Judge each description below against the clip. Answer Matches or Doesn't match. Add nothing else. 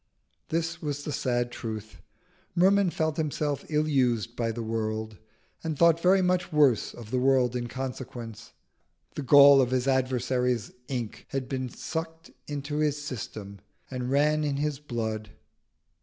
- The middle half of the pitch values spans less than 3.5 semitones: Doesn't match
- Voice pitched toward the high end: Doesn't match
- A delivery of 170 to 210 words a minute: Doesn't match